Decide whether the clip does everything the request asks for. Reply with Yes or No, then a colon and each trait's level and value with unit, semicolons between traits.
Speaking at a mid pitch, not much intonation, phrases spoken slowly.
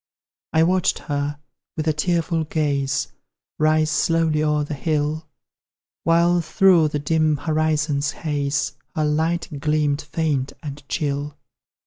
Yes: medium, 155 Hz; narrow, 1.7 semitones; slow, 120 wpm